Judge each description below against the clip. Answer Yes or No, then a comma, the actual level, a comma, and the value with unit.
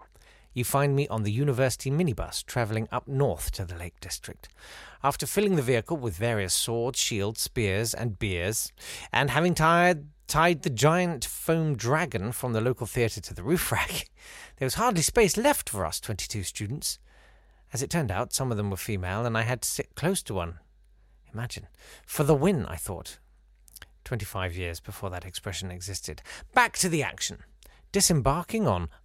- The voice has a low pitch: Yes, low, 120 Hz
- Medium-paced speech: Yes, average, 175 wpm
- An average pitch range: No, wide, 7.3 semitones